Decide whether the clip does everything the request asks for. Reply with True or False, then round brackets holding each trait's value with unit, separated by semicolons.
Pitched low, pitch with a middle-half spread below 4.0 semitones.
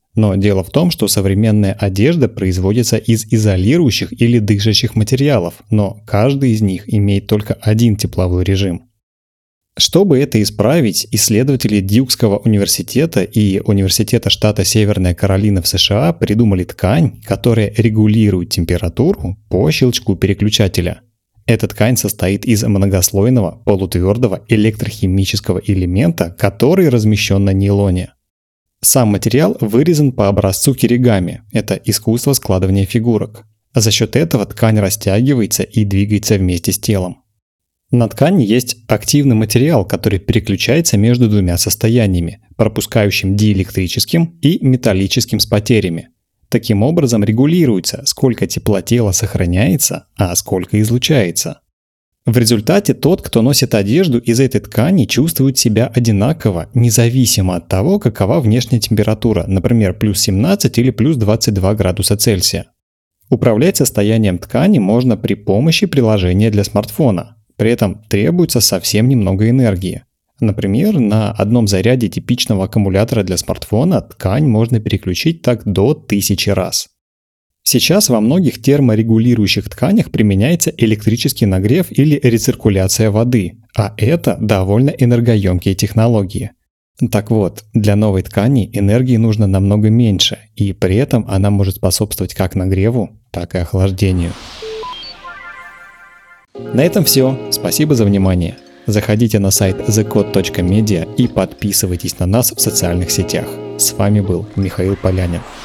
True (110 Hz; 3.6 semitones)